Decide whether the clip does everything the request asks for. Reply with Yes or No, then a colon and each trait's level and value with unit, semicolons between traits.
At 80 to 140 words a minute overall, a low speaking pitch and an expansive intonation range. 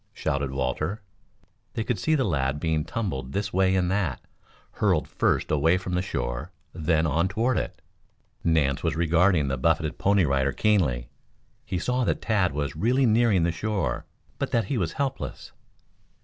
No: average, 165 wpm; very low, 85 Hz; wide, 5.8 semitones